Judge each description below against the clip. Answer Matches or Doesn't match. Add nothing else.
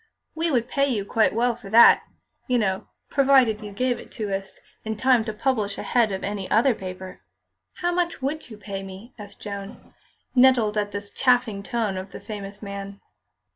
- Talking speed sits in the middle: Matches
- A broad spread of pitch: Doesn't match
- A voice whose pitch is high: Matches